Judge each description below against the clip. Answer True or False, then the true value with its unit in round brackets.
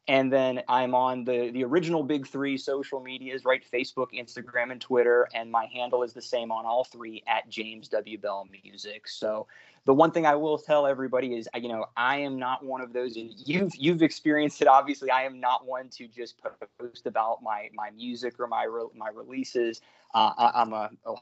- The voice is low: True (125 Hz)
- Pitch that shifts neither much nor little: False (2.3 semitones)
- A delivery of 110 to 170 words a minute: False (205 wpm)